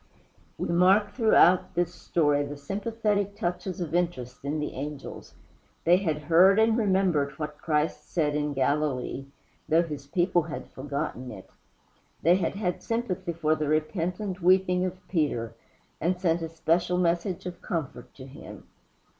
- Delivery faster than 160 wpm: No, average, 150 wpm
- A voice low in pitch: No, medium, 170 Hz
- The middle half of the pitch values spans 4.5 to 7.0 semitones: No, average, 3.7 semitones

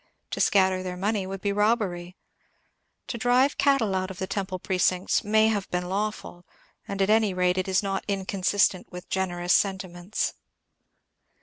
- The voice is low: No, high, 190 Hz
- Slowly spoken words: No, average, 160 wpm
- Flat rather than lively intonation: Yes, narrow, 2.2 semitones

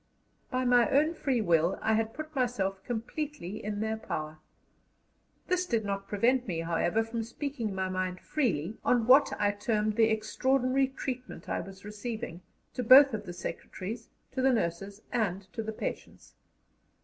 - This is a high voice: Yes, high, 220 Hz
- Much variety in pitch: No, average, 4.5 semitones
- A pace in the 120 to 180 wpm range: Yes, average, 160 wpm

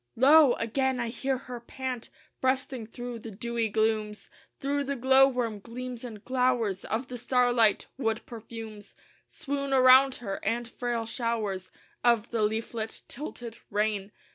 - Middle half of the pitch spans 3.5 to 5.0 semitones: No, narrow, 2.6 semitones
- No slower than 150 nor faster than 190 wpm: No, average, 140 wpm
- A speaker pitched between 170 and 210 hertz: No, high, 235 Hz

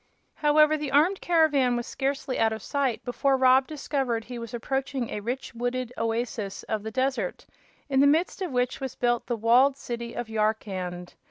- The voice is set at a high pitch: Yes, very high, 250 Hz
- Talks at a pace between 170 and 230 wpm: Yes, average, 180 wpm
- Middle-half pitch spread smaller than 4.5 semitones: Yes, average, 3.3 semitones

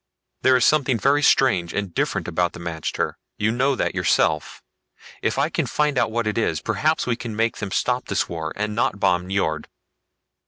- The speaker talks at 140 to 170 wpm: No, average, 195 wpm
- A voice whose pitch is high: No, low, 105 Hz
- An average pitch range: No, wide, 6.1 semitones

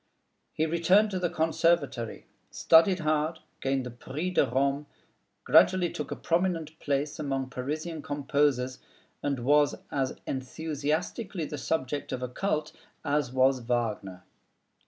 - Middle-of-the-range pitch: Yes, medium, 145 Hz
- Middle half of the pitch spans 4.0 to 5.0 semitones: No, average, 3.6 semitones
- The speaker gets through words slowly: Yes, slow, 130 wpm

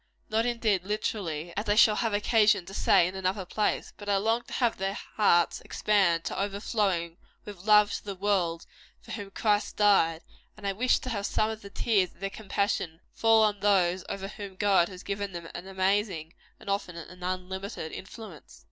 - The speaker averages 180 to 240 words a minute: Yes, average, 190 wpm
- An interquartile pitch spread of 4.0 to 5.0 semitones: No, narrow, 2.4 semitones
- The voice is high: Yes, high, 200 Hz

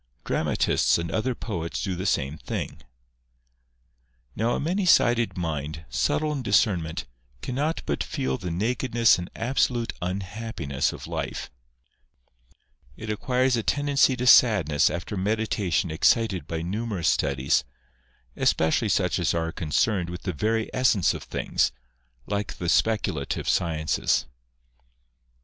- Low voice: Yes, low, 100 Hz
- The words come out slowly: Yes, slow, 125 wpm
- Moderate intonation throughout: No, wide, 6.0 semitones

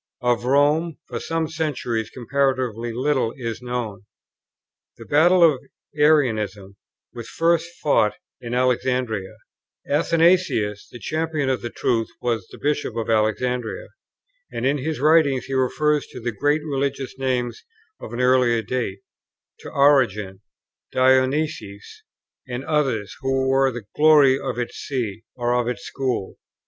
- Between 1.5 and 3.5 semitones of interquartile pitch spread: No, average, 3.9 semitones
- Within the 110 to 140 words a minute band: Yes, slow, 135 wpm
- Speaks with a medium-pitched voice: No, low, 130 Hz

